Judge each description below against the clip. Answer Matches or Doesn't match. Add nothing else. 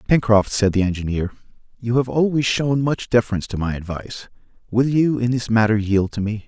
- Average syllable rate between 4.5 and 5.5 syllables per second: Doesn't match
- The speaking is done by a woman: Doesn't match